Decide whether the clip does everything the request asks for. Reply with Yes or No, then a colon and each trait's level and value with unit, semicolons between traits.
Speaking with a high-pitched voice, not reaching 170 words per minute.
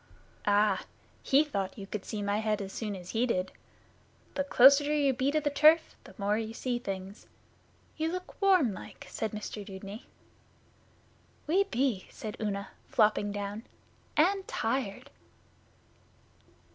Yes: high, 220 Hz; average, 145 wpm